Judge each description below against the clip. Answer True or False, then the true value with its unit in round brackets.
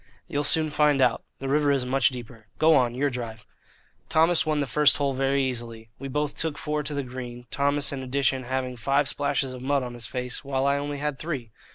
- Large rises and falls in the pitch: False (2.6 semitones)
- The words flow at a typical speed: False (220 wpm)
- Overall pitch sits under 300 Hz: True (135 Hz)